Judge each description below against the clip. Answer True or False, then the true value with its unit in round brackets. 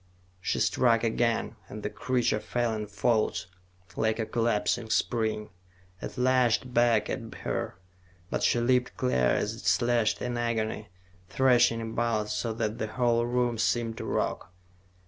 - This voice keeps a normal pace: True (145 wpm)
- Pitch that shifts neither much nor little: False (1.8 semitones)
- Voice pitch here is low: True (115 Hz)